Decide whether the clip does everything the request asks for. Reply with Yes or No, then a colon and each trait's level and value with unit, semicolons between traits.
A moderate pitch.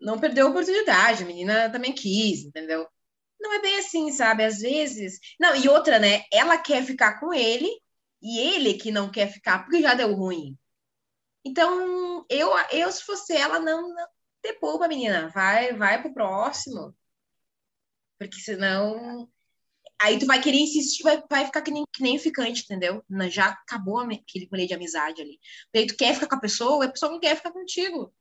No: high, 245 Hz